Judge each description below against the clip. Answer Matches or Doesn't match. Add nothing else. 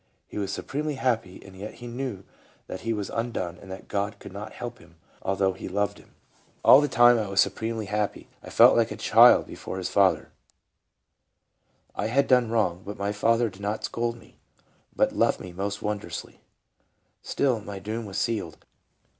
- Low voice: Matches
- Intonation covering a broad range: Doesn't match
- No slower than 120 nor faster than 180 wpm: Doesn't match